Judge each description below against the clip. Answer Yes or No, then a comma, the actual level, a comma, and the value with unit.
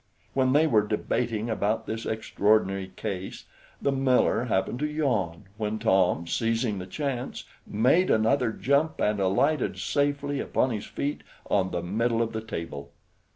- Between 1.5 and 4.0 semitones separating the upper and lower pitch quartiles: No, average, 5.1 semitones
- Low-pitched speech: Yes, low, 110 Hz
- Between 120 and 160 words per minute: Yes, average, 150 wpm